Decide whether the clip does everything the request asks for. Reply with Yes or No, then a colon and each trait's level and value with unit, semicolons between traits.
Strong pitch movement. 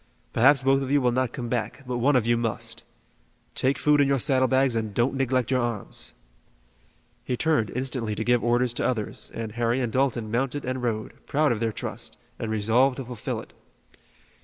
No: narrow, 2.5 semitones